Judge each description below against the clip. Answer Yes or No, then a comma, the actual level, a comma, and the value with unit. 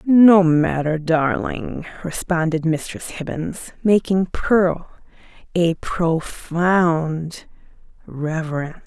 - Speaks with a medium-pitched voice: Yes, medium, 165 Hz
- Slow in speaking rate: Yes, slow, 75 wpm